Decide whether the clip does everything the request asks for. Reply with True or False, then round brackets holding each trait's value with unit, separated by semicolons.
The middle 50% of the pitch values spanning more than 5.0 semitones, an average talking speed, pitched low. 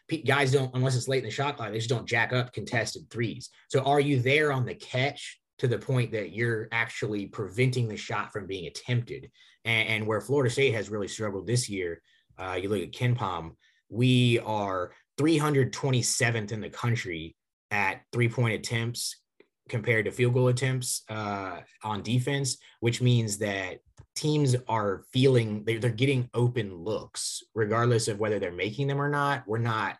False (3.1 semitones; 180 wpm; 120 Hz)